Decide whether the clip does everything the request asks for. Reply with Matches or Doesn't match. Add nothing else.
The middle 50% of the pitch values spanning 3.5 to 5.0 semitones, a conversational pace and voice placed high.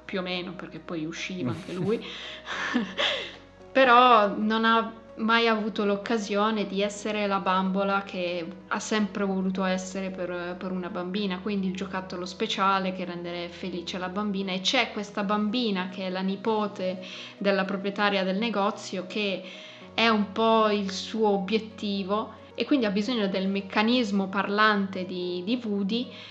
Doesn't match